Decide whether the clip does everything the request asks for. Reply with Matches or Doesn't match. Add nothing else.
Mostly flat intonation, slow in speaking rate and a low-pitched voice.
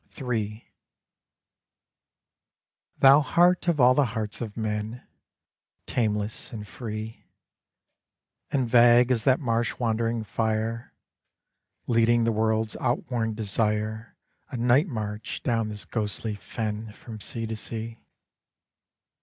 Matches